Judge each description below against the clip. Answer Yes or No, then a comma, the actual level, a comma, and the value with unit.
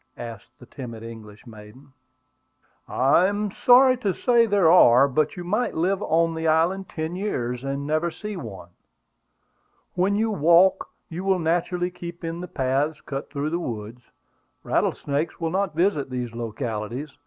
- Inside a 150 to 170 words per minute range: Yes, average, 155 wpm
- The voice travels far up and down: Yes, wide, 6.0 semitones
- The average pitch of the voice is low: No, medium, 160 Hz